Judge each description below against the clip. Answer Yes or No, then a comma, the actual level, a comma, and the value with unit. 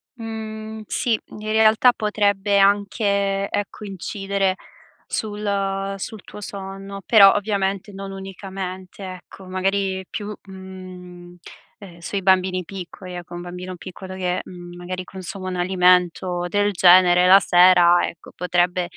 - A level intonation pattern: Yes, narrow, 1.8 semitones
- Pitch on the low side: No, high, 190 Hz